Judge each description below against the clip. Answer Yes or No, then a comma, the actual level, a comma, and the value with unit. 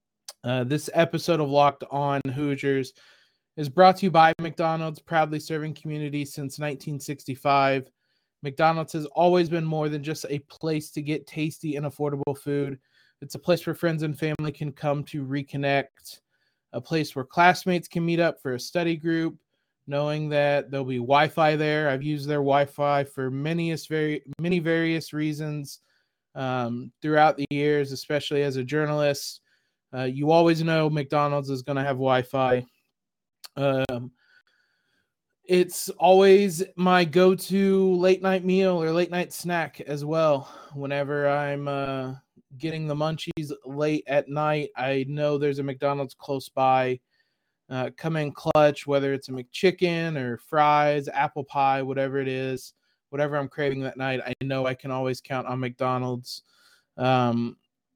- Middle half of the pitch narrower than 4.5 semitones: Yes, average, 2.8 semitones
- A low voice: No, medium, 145 Hz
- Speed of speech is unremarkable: Yes, average, 155 wpm